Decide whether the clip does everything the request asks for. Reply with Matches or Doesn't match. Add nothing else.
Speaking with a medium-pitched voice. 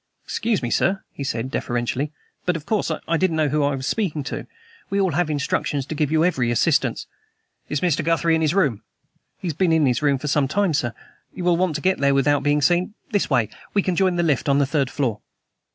Matches